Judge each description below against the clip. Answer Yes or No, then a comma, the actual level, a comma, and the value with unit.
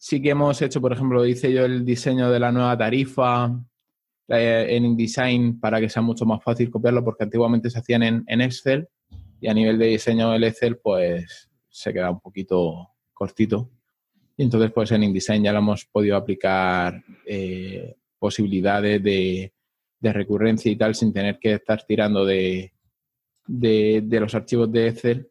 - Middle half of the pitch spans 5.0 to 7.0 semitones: No, average, 2.9 semitones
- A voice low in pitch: Yes, low, 115 Hz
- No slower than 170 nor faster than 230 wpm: Yes, average, 175 wpm